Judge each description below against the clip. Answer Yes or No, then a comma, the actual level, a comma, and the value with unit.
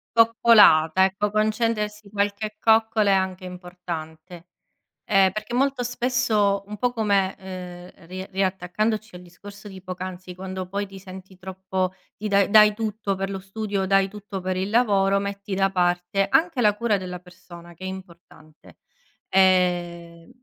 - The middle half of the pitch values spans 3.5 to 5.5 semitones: No, narrow, 2.4 semitones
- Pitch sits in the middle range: No, high, 195 Hz